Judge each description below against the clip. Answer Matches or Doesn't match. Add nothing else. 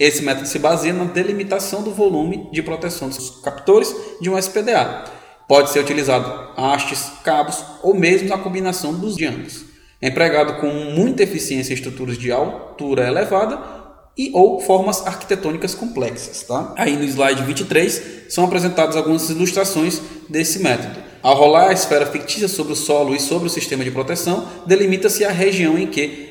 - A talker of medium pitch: Matches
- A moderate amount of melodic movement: Matches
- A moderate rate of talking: Matches